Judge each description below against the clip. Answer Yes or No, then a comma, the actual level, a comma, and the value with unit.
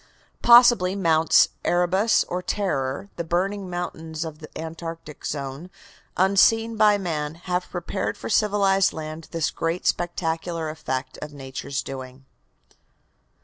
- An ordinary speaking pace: No, slow, 125 wpm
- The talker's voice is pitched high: No, medium, 170 Hz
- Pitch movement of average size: Yes, average, 3.8 semitones